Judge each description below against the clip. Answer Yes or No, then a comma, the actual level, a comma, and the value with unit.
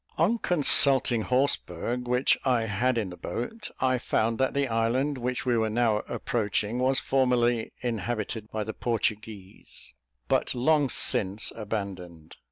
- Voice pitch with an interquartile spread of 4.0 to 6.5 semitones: No, average, 3.1 semitones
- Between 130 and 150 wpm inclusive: Yes, average, 140 wpm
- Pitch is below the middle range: Yes, low, 120 Hz